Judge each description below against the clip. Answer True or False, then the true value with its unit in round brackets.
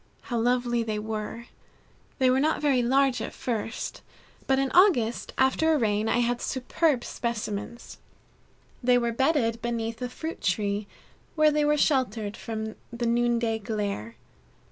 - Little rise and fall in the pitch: False (3.1 semitones)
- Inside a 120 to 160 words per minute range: True (145 wpm)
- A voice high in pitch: True (240 Hz)